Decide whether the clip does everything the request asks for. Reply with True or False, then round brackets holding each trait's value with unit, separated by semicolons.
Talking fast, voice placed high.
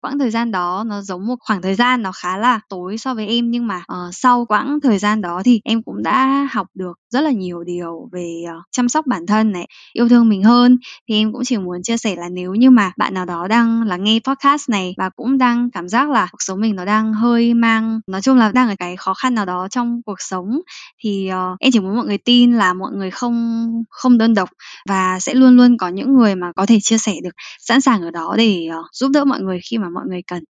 True (265 wpm; 220 Hz)